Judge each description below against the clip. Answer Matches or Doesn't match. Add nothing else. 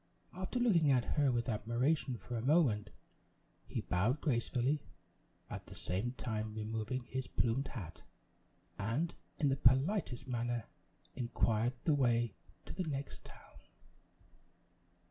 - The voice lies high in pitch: Doesn't match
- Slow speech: Matches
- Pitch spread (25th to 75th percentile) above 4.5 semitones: Doesn't match